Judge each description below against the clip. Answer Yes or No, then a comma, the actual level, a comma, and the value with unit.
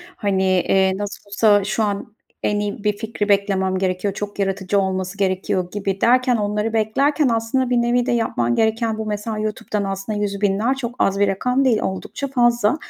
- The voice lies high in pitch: Yes, high, 205 Hz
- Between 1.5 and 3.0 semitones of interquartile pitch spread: Yes, average, 2.7 semitones